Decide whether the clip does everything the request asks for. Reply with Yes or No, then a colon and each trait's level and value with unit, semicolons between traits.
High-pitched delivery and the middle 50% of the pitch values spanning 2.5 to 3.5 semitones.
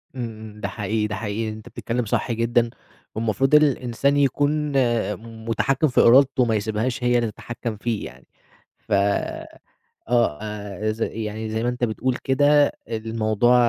No: low, 115 Hz; average, 2.9 semitones